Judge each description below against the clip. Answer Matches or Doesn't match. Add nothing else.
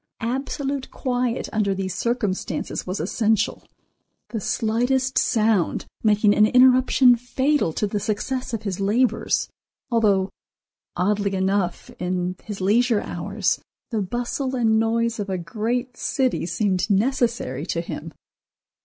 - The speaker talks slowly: Matches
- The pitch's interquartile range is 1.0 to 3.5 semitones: Doesn't match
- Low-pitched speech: Doesn't match